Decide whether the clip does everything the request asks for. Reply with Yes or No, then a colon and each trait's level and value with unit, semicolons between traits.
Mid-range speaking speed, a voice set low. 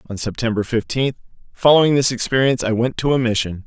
Yes: average, 180 wpm; low, 120 Hz